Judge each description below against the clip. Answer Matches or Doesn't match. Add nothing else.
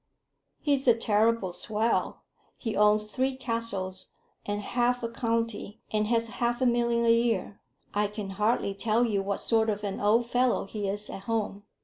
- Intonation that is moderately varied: Doesn't match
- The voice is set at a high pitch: Matches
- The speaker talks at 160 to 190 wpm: Matches